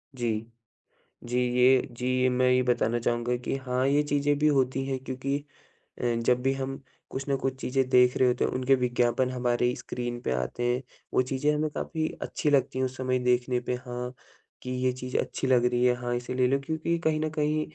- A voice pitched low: Yes, low, 130 Hz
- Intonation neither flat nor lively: No, narrow, 1.6 semitones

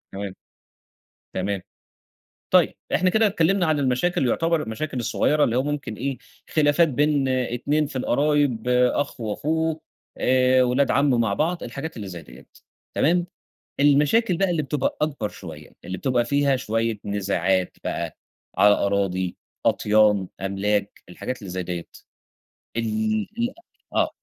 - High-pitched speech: No, low, 125 Hz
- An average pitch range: No, wide, 6.4 semitones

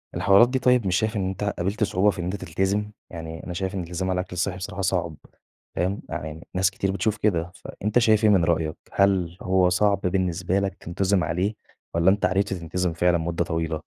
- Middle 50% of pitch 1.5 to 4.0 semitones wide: Yes, narrow, 2.4 semitones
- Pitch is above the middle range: No, very low, 95 Hz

